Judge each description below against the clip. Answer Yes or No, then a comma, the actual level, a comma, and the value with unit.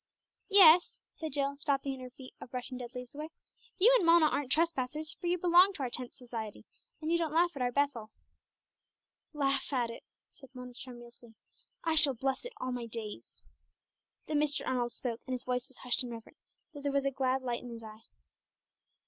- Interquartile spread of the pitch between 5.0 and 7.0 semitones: No, average, 3.7 semitones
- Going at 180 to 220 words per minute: Yes, average, 200 wpm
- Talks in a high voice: Yes, very high, 265 Hz